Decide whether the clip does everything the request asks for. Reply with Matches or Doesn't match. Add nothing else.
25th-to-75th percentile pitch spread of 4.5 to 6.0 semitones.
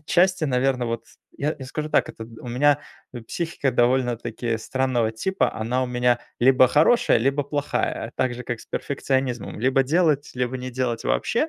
Doesn't match